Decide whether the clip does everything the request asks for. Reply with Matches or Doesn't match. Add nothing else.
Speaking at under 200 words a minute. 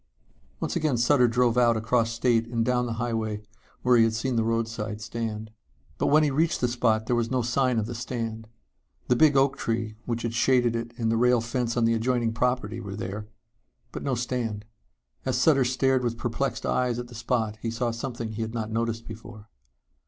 Doesn't match